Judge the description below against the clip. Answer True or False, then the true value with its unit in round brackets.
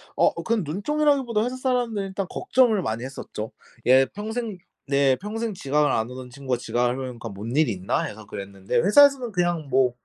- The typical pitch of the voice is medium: True (150 Hz)